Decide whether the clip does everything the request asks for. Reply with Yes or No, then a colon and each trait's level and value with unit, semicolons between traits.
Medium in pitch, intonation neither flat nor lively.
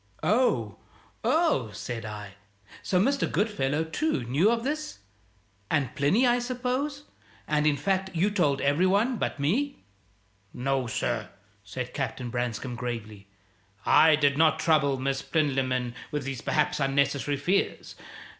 No: medium, 145 Hz; wide, 7.7 semitones